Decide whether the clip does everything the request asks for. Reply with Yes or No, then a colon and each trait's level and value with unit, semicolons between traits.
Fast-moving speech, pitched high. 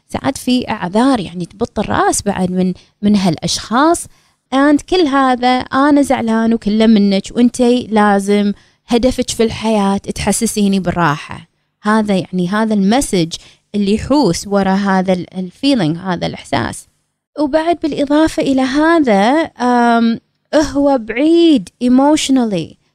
No: average, 110 wpm; high, 225 Hz